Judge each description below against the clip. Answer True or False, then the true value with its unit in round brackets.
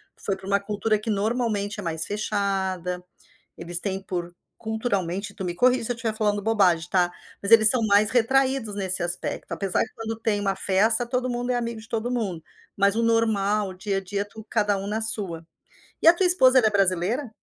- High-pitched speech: True (210 Hz)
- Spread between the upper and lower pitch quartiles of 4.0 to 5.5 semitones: False (2.9 semitones)